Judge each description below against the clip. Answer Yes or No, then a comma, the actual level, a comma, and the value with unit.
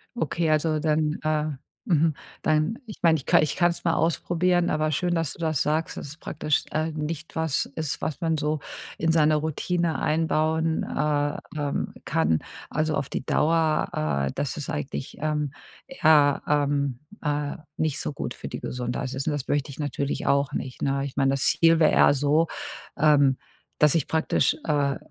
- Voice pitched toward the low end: No, medium, 150 Hz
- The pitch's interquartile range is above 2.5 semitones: No, narrow, 2.0 semitones